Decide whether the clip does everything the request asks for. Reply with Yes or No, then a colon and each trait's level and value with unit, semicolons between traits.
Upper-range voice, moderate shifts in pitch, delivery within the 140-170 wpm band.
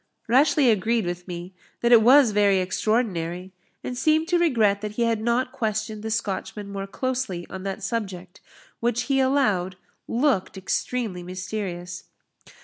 Yes: high, 215 Hz; average, 4.6 semitones; average, 145 wpm